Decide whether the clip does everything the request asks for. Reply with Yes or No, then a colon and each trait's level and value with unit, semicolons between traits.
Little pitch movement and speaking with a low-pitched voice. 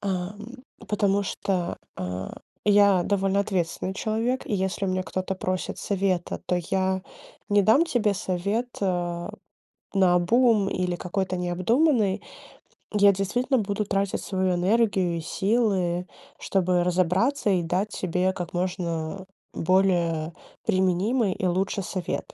No: narrow, 2.2 semitones; high, 190 Hz